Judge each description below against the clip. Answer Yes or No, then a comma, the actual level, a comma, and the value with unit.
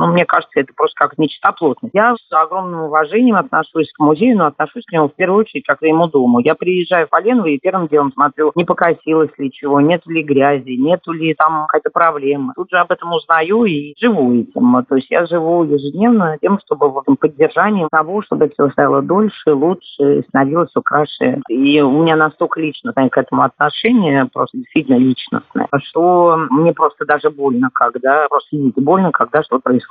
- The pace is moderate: No, fast, 190 wpm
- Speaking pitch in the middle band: Yes, medium, 160 Hz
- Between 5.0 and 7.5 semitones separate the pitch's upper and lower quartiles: No, average, 3.9 semitones